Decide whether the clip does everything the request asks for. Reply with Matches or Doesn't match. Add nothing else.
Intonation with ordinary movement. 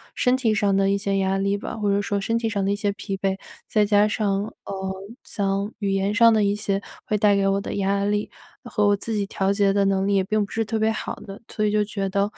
Doesn't match